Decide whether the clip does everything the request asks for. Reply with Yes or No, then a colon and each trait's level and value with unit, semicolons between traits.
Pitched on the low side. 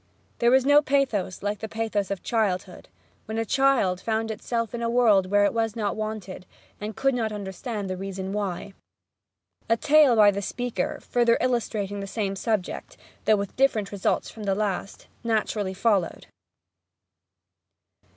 No: high, 215 Hz